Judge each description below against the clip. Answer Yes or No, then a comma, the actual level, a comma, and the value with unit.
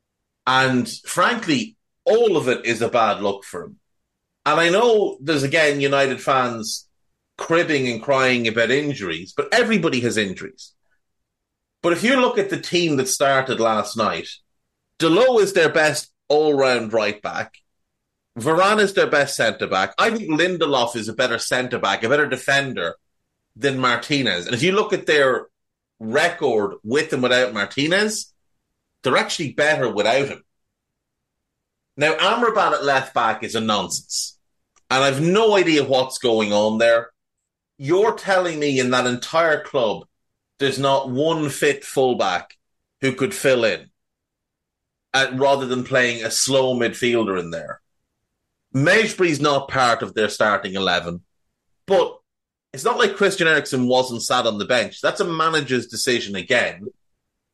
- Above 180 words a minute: No, average, 150 wpm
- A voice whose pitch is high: No, low, 135 Hz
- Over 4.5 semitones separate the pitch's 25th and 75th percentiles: Yes, average, 5.2 semitones